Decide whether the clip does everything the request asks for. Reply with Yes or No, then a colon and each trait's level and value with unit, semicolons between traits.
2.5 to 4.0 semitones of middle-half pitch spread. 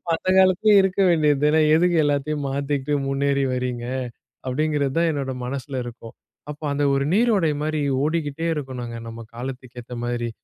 Yes: average, 3.2 semitones